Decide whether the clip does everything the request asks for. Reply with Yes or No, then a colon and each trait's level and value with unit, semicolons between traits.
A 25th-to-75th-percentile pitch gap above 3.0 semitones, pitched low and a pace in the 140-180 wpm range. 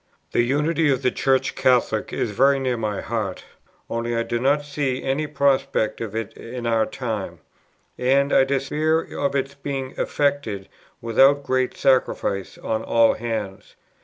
Yes: average, 3.4 semitones; low, 130 Hz; average, 155 wpm